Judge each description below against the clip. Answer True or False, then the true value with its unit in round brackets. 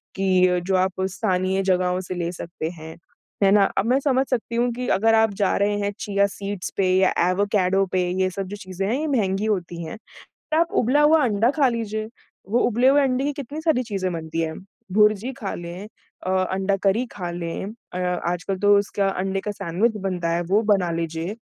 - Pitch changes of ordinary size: True (3.5 semitones)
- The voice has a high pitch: True (195 Hz)